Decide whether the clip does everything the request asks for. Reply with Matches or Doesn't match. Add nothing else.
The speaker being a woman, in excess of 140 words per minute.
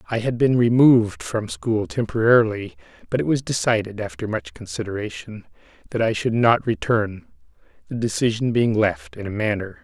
Doesn't match